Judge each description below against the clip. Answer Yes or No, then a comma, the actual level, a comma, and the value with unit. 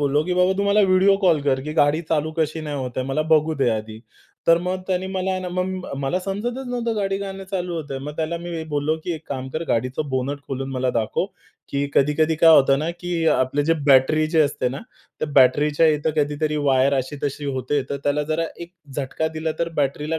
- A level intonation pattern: No, average, 4.1 semitones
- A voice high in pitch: No, medium, 155 Hz